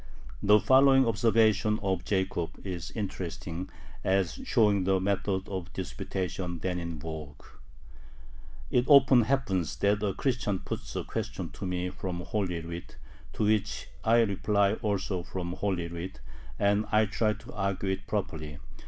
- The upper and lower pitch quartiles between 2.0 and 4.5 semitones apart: Yes, average, 3.1 semitones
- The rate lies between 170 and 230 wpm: No, average, 145 wpm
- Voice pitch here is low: Yes, very low, 95 Hz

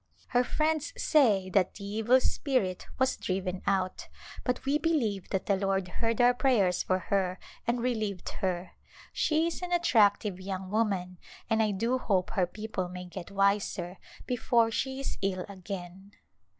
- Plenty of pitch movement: No, average, 4.8 semitones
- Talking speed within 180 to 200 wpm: No, average, 165 wpm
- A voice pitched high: Yes, high, 200 Hz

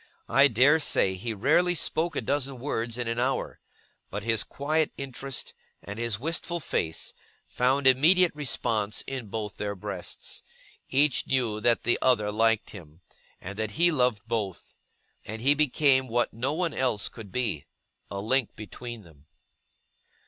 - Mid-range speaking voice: No, low, 120 Hz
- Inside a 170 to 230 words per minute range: No, average, 155 wpm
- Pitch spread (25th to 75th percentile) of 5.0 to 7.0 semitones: No, average, 4.5 semitones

